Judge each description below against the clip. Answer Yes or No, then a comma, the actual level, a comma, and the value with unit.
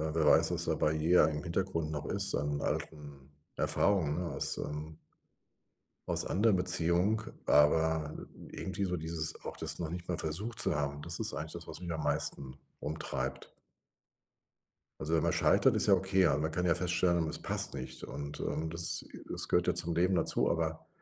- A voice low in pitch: Yes, very low, 80 Hz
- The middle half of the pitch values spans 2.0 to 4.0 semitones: Yes, average, 2.7 semitones